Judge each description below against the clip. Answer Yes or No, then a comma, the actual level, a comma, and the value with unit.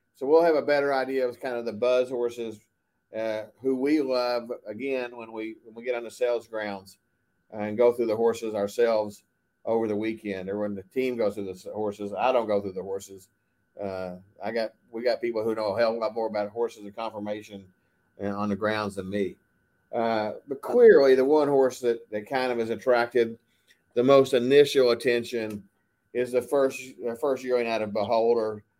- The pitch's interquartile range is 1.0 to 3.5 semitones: Yes, average, 2.9 semitones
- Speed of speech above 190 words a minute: Yes, fast, 205 wpm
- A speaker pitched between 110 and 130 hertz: Yes, low, 115 Hz